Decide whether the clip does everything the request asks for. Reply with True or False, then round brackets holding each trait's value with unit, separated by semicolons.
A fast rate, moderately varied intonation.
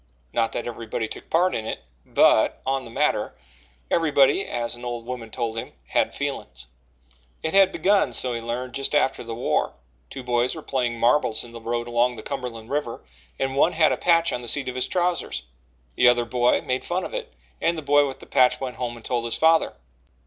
True (215 wpm; 3.8 semitones)